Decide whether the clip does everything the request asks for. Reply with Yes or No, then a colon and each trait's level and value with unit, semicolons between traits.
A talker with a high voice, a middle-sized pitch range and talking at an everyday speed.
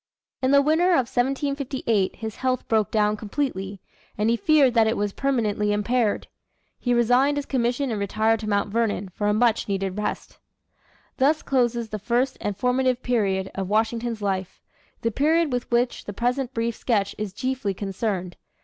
Yes: high, 230 Hz; average, 3.8 semitones; average, 170 wpm